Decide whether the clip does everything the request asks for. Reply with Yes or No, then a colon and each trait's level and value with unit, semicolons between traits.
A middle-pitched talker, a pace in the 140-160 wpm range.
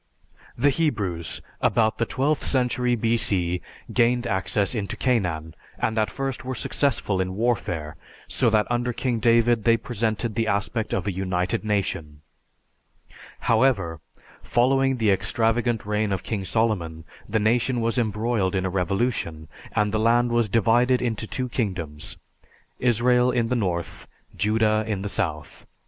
No: low, 110 Hz; average, 145 wpm